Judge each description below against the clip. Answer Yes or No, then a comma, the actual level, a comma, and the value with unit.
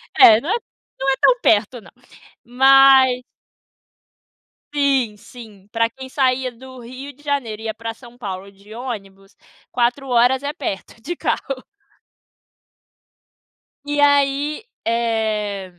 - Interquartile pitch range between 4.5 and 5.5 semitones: No, average, 3.6 semitones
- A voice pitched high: Yes, high, 245 Hz